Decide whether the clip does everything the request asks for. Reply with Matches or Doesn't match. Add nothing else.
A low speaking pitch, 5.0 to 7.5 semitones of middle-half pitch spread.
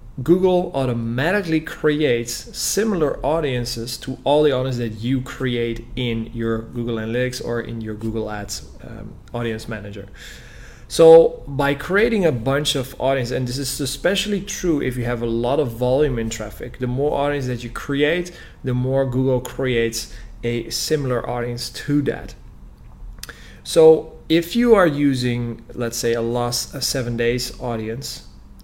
Doesn't match